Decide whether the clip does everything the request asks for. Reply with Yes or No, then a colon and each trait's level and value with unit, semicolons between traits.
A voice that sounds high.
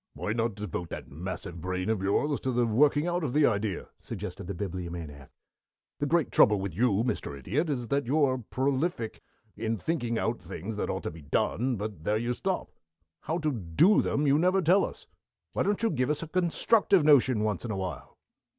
No: low, 120 Hz